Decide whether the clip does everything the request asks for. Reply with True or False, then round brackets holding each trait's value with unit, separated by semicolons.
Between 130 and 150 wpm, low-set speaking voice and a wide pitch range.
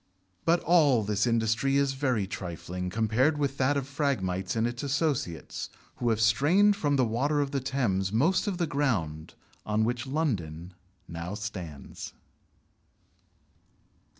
True (140 wpm; 120 Hz; 6.1 semitones)